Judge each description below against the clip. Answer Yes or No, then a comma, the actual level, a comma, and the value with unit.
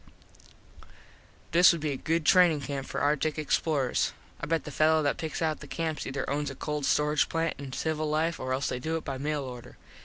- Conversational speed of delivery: No, fast, 215 wpm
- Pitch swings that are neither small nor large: No, narrow, 2.2 semitones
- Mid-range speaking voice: Yes, medium, 150 Hz